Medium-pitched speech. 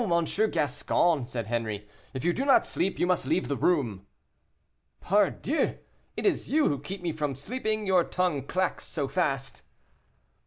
Yes: medium, 170 Hz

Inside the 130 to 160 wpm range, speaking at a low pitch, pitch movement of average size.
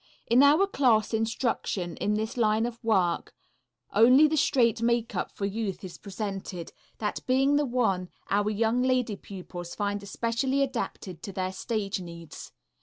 No: average, 150 wpm; high, 220 Hz; average, 4.1 semitones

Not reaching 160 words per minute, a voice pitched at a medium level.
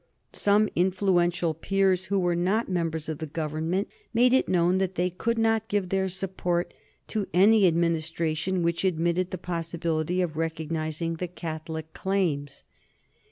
Yes: average, 145 wpm; medium, 175 Hz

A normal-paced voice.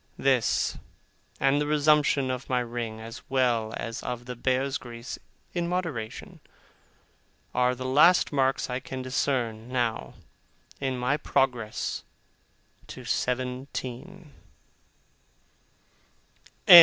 No: slow, 105 wpm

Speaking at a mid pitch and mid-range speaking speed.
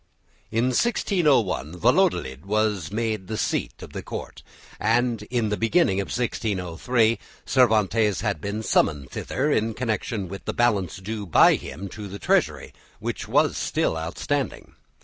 No: low, 110 Hz; average, 145 wpm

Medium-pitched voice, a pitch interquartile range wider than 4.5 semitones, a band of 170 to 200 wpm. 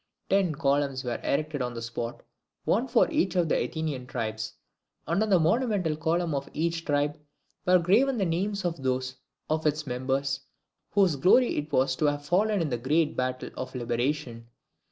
Yes: medium, 150 Hz; average, 5.2 semitones; average, 175 wpm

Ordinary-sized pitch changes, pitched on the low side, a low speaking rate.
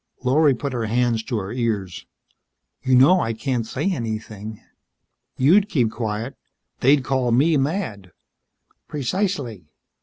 Yes: average, 4.2 semitones; low, 125 Hz; slow, 125 wpm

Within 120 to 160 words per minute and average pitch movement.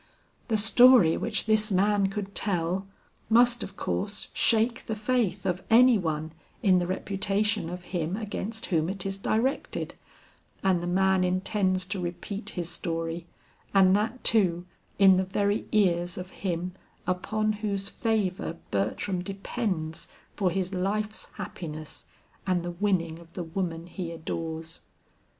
Yes: average, 140 wpm; average, 3.2 semitones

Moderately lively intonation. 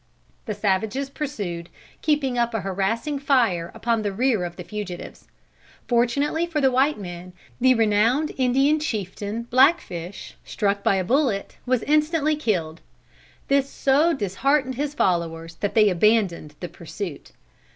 No: wide, 6.4 semitones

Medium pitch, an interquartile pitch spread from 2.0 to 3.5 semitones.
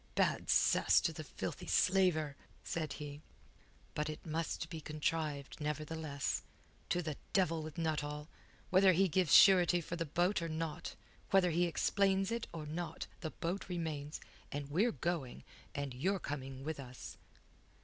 Yes: medium, 160 Hz; average, 3.0 semitones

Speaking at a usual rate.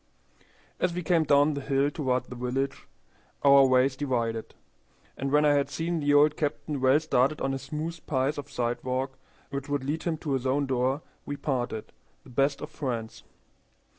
Yes: average, 180 wpm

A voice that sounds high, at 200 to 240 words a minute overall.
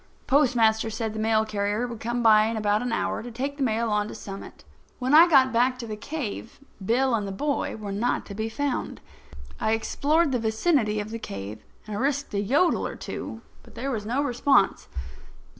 Yes: high, 230 Hz; fast, 205 wpm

